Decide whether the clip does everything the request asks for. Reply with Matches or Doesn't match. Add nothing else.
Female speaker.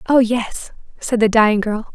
Matches